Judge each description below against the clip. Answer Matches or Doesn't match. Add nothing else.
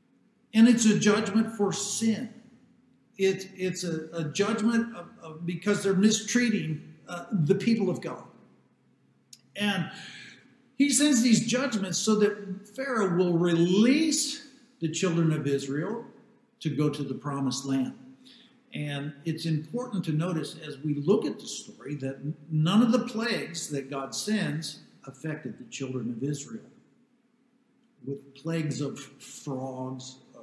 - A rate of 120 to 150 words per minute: Matches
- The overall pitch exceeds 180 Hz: Matches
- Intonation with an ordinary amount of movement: Doesn't match